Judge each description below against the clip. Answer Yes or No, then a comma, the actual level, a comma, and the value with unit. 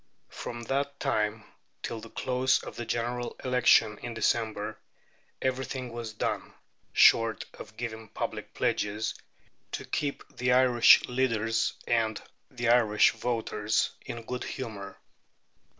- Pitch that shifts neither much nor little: No, narrow, 2.2 semitones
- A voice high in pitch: No, low, 115 Hz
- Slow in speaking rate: Yes, slow, 120 wpm